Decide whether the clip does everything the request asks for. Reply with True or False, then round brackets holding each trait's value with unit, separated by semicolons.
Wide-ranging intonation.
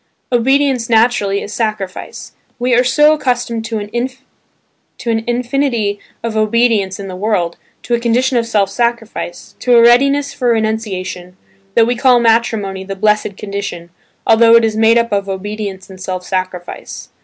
False (3.3 semitones)